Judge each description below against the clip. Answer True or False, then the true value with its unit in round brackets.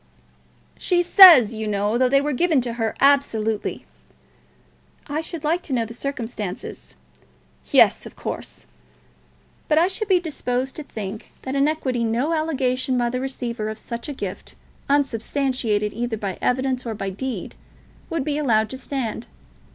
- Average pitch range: True (4.3 semitones)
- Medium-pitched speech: False (255 Hz)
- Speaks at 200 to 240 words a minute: False (160 wpm)